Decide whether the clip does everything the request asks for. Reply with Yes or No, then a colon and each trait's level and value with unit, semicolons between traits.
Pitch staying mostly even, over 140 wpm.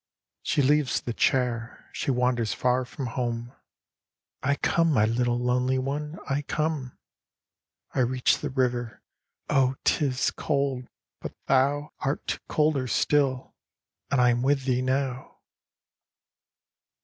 No: narrow, 2.2 semitones; slow, 135 wpm